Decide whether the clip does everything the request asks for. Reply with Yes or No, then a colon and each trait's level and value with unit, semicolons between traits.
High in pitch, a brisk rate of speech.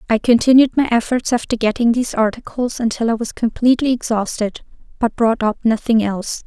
No: high, 230 Hz; average, 165 wpm